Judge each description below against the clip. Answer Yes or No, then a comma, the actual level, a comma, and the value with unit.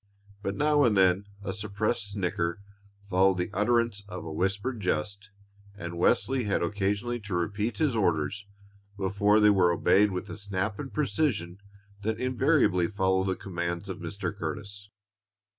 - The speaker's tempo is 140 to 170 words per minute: Yes, average, 150 wpm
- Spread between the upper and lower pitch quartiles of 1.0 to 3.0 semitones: Yes, average, 2.7 semitones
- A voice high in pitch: No, low, 100 Hz